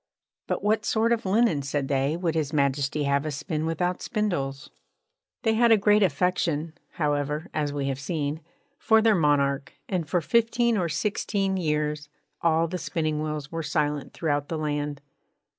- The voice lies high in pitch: No, medium, 155 Hz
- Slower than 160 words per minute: No, average, 165 wpm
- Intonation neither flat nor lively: Yes, average, 4.3 semitones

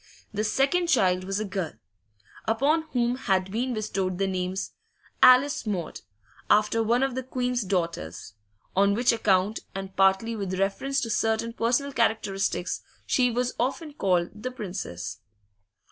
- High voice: Yes, high, 215 Hz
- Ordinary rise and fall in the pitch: Yes, average, 4.5 semitones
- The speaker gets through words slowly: No, average, 145 wpm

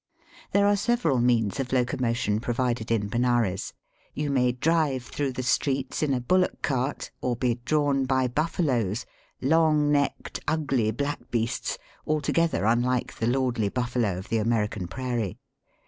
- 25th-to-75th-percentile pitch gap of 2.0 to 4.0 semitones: Yes, average, 3.5 semitones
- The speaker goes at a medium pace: Yes, average, 150 wpm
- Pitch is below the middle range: Yes, low, 125 Hz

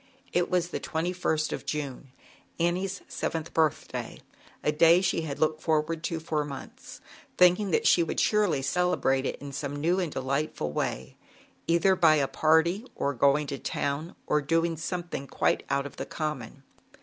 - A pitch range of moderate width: Yes, average, 3.4 semitones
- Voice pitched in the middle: Yes, medium, 155 Hz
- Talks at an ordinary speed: Yes, average, 170 wpm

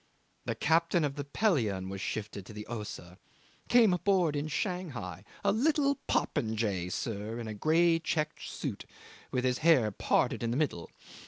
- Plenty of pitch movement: Yes, wide, 8.2 semitones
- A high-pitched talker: No, low, 135 Hz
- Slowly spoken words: No, average, 160 wpm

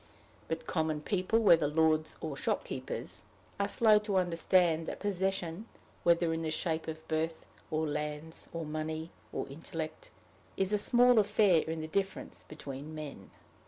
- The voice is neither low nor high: Yes, medium, 165 Hz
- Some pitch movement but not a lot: Yes, average, 3.5 semitones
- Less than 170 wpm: Yes, average, 150 wpm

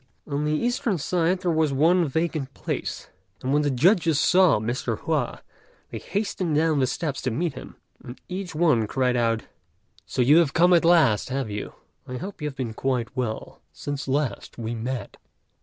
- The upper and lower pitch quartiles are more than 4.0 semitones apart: Yes, average, 5.1 semitones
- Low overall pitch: No, medium, 145 Hz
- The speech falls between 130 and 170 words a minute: No, average, 185 wpm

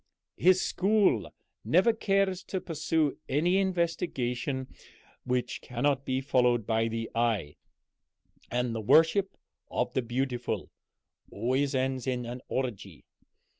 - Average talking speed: No, slow, 115 wpm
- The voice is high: No, low, 130 Hz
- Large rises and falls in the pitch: Yes, wide, 5.8 semitones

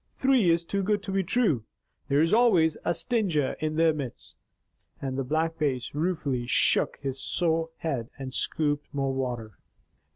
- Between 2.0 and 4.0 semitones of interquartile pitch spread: No, average, 4.7 semitones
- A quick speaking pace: No, average, 165 wpm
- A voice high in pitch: No, medium, 155 Hz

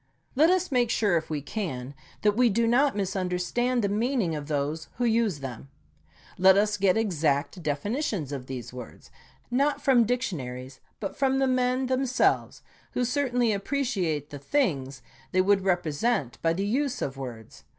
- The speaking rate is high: No, average, 165 wpm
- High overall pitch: Yes, high, 200 Hz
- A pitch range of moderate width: No, wide, 9.0 semitones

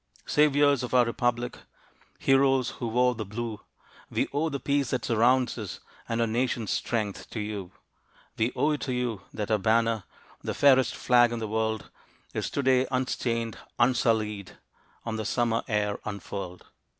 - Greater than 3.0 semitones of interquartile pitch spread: No, average, 2.7 semitones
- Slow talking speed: No, average, 160 wpm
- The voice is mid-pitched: No, low, 115 Hz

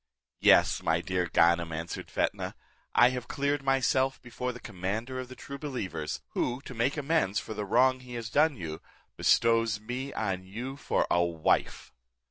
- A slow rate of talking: No, average, 170 wpm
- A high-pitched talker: No, low, 120 Hz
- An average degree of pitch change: No, wide, 5.9 semitones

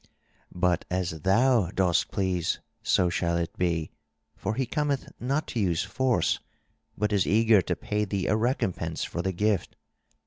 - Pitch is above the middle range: No, very low, 95 Hz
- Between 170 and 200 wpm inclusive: No, average, 160 wpm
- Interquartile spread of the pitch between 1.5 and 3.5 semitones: No, average, 4.2 semitones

